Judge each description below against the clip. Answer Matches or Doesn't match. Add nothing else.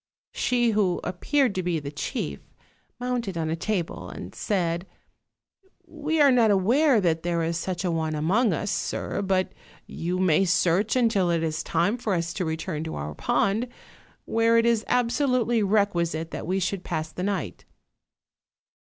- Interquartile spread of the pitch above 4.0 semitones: Matches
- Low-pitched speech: Doesn't match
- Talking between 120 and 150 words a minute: Doesn't match